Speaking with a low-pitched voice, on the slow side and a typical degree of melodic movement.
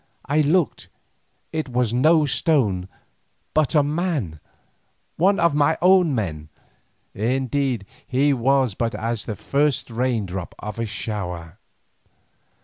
No: low, 130 Hz; slow, 125 wpm; wide, 5.8 semitones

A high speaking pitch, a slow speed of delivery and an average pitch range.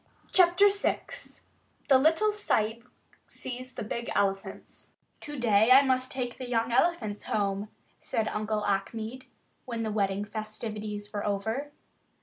Yes: high, 225 Hz; slow, 130 wpm; average, 3.8 semitones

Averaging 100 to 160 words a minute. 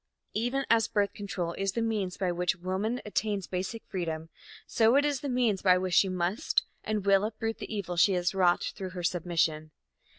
No: average, 195 wpm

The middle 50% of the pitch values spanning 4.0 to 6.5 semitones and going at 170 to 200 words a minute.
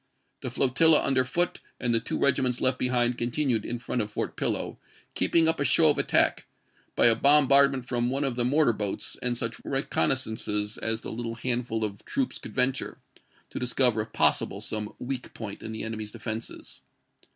No: average, 3.2 semitones; average, 185 wpm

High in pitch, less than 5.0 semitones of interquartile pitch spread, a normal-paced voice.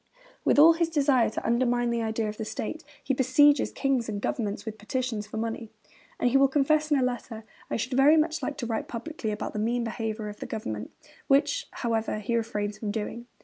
No: high, 235 Hz; average, 3.8 semitones; fast, 215 wpm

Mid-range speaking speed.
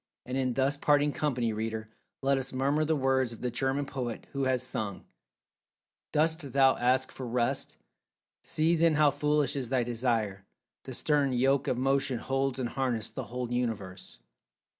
Yes: average, 165 wpm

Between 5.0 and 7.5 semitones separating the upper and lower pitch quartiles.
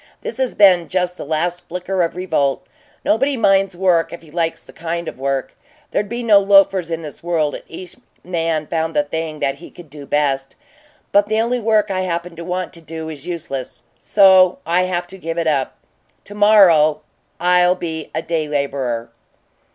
No: average, 3.2 semitones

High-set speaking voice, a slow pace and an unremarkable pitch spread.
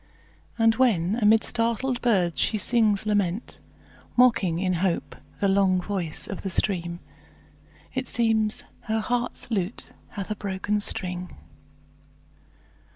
Yes: high, 205 Hz; slow, 120 wpm; average, 3.5 semitones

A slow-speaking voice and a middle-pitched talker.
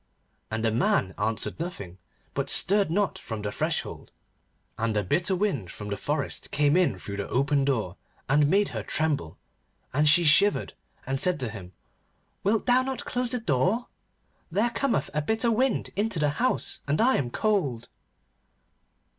No: average, 165 wpm; medium, 150 Hz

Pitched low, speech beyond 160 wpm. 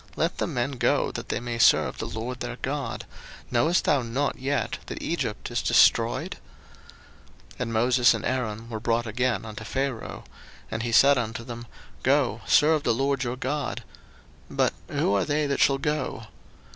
Yes: low, 125 Hz; average, 170 wpm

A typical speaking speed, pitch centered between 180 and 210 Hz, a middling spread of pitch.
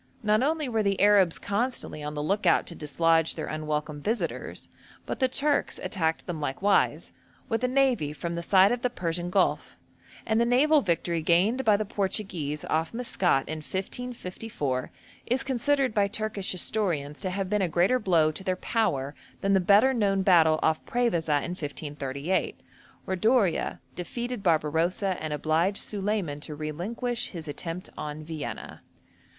No: average, 160 wpm; medium, 185 Hz; wide, 5.7 semitones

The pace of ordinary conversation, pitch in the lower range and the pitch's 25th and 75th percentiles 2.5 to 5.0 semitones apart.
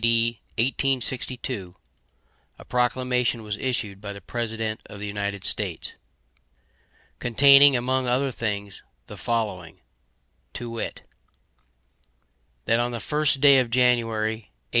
No: slow, 120 wpm; low, 115 Hz; average, 2.9 semitones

